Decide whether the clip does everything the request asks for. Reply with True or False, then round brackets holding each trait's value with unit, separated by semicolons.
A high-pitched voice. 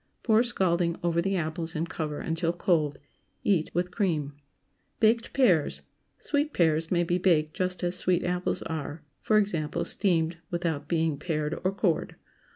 False (170 Hz)